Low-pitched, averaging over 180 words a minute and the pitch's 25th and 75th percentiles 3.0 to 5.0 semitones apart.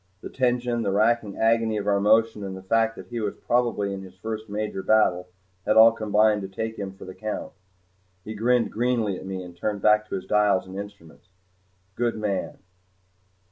No: low, 105 Hz; average, 195 wpm; narrow, 2.5 semitones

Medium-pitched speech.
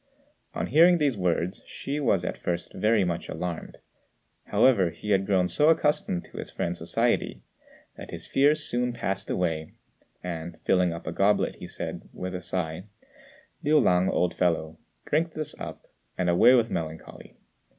No: very low, 90 Hz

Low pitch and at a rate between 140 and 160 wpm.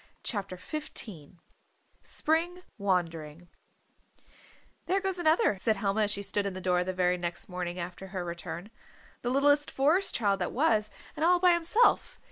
No: high, 200 Hz; average, 155 wpm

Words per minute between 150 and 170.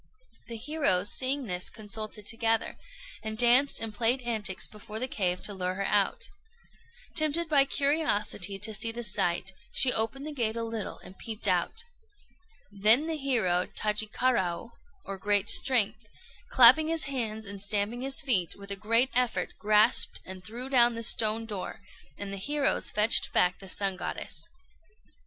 Yes: average, 160 wpm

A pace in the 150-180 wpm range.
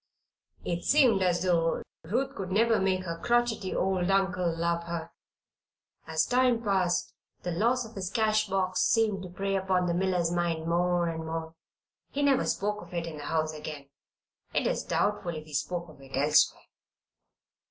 Yes: average, 175 wpm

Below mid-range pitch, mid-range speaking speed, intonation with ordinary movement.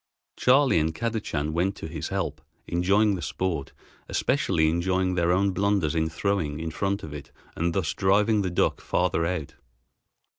Yes: very low, 90 Hz; average, 160 wpm; average, 3.8 semitones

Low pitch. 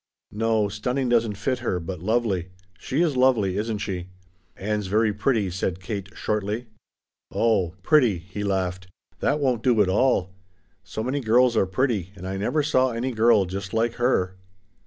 Yes: low, 105 Hz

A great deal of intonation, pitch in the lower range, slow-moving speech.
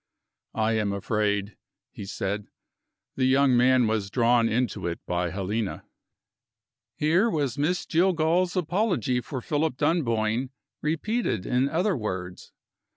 Yes: wide, 6.8 semitones; low, 125 Hz; slow, 120 wpm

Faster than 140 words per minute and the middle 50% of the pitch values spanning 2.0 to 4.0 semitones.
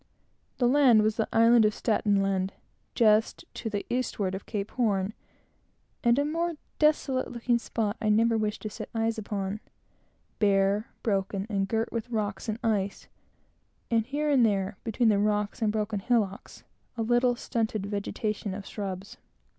Yes: average, 160 wpm; average, 2.7 semitones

